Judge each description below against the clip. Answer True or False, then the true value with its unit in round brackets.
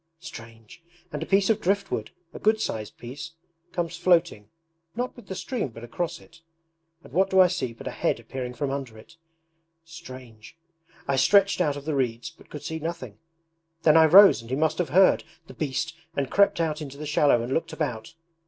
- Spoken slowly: False (200 wpm)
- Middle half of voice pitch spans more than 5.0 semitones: True (5.4 semitones)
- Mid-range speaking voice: True (155 Hz)